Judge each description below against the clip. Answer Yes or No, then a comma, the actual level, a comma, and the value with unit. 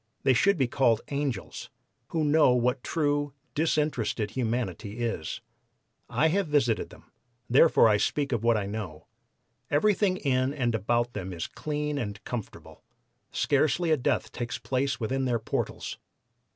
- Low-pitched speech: Yes, low, 130 Hz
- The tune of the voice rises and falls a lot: No, average, 4.5 semitones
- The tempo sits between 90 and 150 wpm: Yes, average, 145 wpm